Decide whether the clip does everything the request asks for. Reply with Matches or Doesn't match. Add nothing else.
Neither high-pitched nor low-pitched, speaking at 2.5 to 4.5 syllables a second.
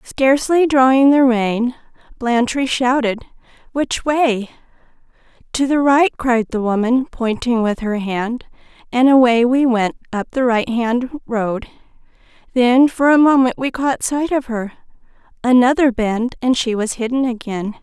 Doesn't match